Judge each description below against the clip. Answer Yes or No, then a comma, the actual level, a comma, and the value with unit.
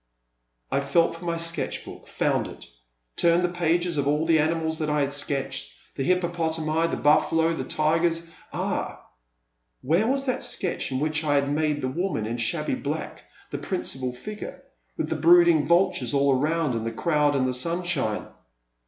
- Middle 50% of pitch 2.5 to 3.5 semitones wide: Yes, average, 3.2 semitones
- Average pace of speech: Yes, average, 180 wpm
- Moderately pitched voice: Yes, medium, 160 Hz